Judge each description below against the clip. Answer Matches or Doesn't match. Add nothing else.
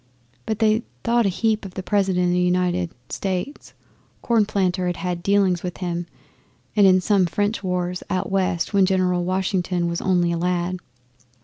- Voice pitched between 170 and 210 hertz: Matches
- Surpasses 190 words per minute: Doesn't match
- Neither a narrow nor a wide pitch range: Doesn't match